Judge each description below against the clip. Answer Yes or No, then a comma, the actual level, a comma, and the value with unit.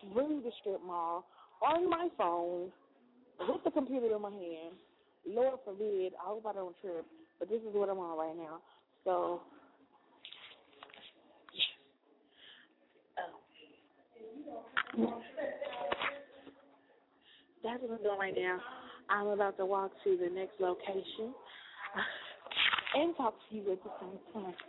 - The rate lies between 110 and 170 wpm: Yes, slow, 135 wpm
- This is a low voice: No, high, 200 Hz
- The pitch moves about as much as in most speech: No, wide, 5.7 semitones